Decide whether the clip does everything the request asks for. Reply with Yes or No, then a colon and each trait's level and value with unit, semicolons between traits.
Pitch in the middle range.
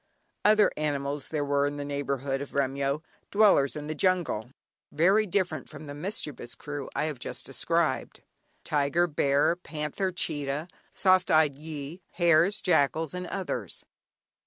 Yes: medium, 150 Hz